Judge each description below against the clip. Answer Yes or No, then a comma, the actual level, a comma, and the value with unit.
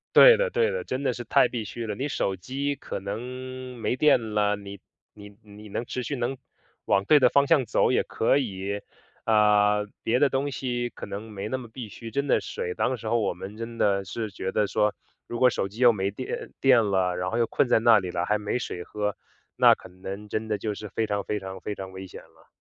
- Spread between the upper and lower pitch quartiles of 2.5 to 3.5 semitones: No, average, 4.0 semitones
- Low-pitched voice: Yes, low, 110 Hz